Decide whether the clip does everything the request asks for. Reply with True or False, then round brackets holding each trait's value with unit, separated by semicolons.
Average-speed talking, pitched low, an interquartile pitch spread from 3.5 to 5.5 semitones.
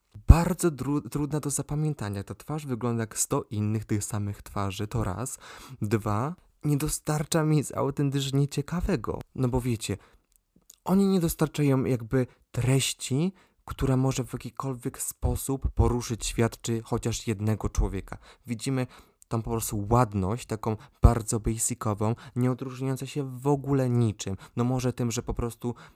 True (140 wpm; 125 Hz; 3.9 semitones)